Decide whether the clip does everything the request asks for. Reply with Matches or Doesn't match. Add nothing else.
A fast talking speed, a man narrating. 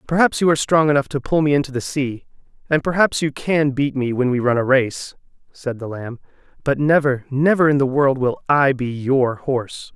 Matches